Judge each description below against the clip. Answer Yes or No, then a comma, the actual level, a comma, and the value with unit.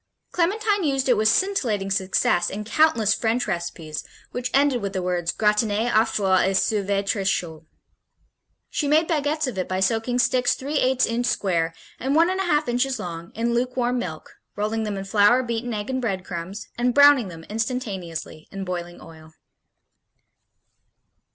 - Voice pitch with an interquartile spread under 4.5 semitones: No, average, 5.1 semitones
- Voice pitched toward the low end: No, high, 220 Hz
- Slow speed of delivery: No, average, 170 wpm